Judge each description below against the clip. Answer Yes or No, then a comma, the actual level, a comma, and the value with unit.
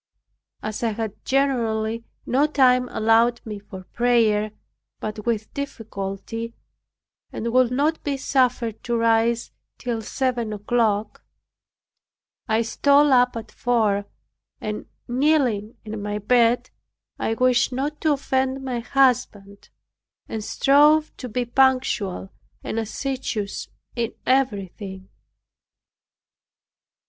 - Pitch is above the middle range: Yes, high, 235 Hz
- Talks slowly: Yes, slow, 110 wpm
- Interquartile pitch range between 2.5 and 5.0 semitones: Yes, average, 3.3 semitones